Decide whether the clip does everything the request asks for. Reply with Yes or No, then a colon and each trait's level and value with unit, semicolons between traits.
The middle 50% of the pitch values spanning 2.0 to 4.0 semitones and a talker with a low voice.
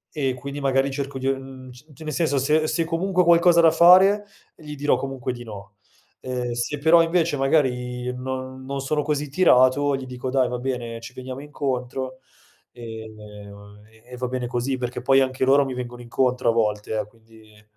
Yes: average, 2.8 semitones; low, 130 Hz